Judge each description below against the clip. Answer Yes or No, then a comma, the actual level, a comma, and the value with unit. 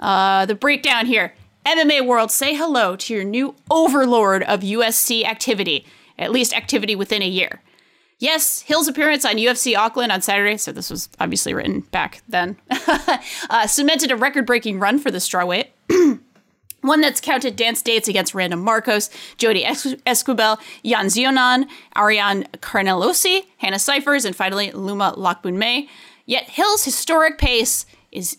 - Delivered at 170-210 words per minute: No, average, 150 wpm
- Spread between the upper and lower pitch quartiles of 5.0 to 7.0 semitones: Yes, wide, 5.6 semitones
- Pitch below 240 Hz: No, high, 245 Hz